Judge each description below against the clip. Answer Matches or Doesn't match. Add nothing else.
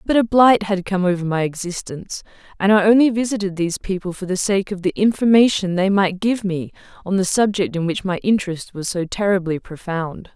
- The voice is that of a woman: Matches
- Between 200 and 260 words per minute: Matches